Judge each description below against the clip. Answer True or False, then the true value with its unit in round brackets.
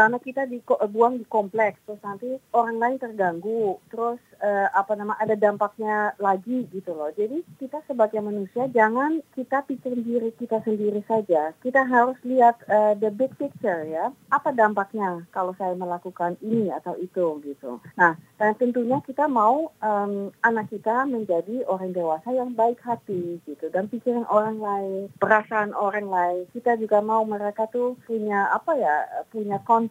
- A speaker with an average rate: False (160 wpm)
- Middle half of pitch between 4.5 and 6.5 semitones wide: False (3.6 semitones)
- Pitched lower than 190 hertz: False (215 Hz)